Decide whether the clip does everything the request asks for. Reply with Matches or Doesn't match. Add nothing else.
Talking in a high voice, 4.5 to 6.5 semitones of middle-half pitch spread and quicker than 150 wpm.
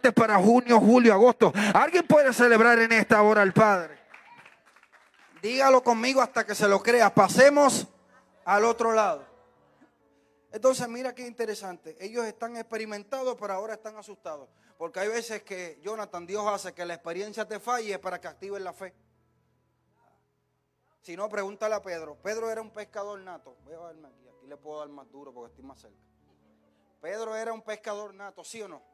Doesn't match